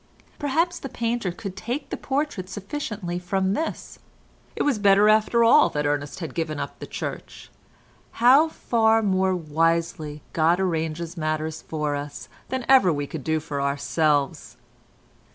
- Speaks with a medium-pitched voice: Yes, medium, 180 Hz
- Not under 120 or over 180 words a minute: Yes, average, 145 wpm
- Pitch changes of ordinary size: No, wide, 6.7 semitones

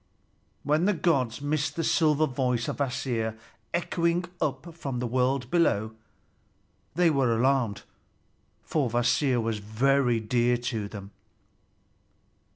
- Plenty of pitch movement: No, average, 4.5 semitones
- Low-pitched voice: Yes, low, 130 Hz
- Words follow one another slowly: Yes, slow, 120 wpm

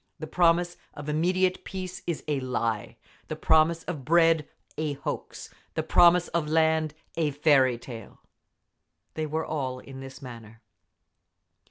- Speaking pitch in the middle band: Yes, medium, 155 Hz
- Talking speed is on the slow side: Yes, slow, 125 wpm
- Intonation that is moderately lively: Yes, average, 4.0 semitones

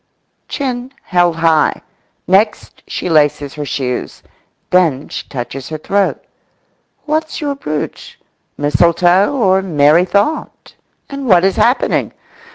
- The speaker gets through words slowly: Yes, slow, 115 wpm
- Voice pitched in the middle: Yes, medium, 180 Hz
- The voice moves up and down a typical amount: No, wide, 6.1 semitones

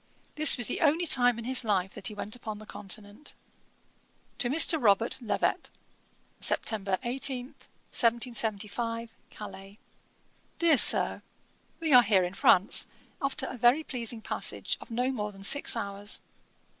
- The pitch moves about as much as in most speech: Yes, average, 3.7 semitones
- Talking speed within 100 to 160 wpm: Yes, average, 145 wpm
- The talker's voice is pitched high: Yes, high, 230 Hz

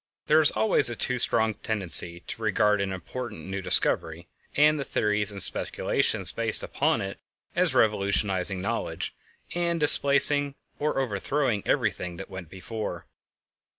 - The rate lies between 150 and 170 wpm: No, average, 140 wpm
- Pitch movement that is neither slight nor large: No, wide, 6.0 semitones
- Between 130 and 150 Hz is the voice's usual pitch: No, low, 105 Hz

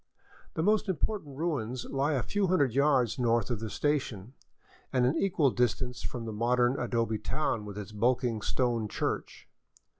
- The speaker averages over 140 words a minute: Yes, average, 160 wpm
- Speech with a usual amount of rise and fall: Yes, average, 4.0 semitones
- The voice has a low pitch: Yes, low, 125 Hz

